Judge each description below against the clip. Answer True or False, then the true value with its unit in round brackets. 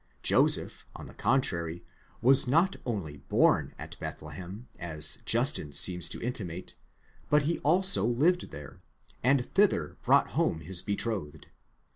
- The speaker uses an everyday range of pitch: False (8.3 semitones)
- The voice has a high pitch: False (110 Hz)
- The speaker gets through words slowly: True (125 wpm)